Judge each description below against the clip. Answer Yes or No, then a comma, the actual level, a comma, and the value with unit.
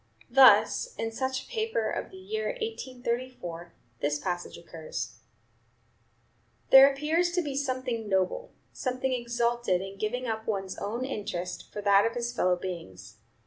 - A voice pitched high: Yes, high, 235 Hz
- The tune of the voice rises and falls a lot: Yes, wide, 6.1 semitones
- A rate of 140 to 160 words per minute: Yes, average, 145 wpm